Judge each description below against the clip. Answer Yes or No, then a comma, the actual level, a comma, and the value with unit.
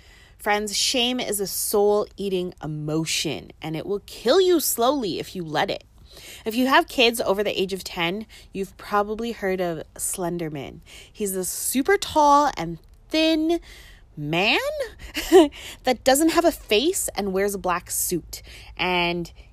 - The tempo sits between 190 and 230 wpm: No, average, 150 wpm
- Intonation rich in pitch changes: Yes, wide, 7.1 semitones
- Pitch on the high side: Yes, high, 205 Hz